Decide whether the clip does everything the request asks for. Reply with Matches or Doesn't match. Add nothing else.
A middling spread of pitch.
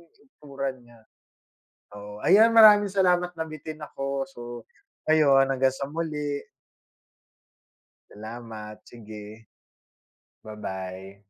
Doesn't match